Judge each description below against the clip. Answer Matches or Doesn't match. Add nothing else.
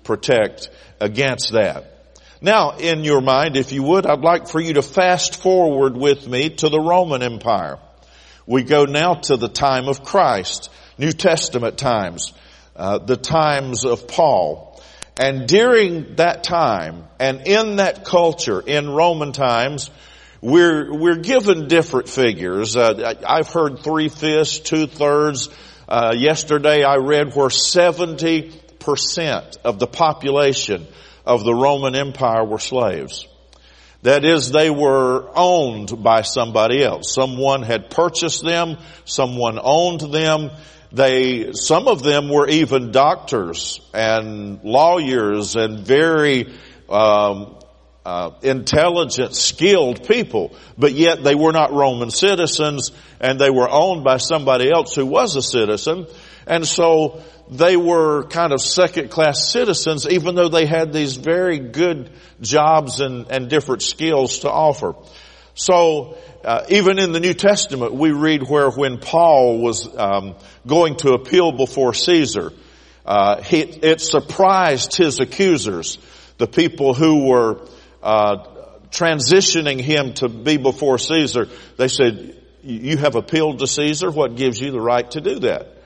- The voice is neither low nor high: Matches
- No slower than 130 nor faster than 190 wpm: Matches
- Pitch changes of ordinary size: Matches